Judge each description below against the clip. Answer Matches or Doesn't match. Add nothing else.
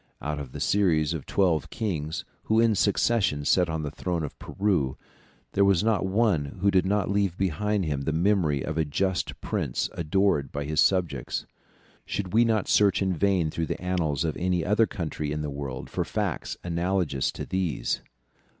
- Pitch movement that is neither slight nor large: Matches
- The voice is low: Matches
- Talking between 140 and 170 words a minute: Doesn't match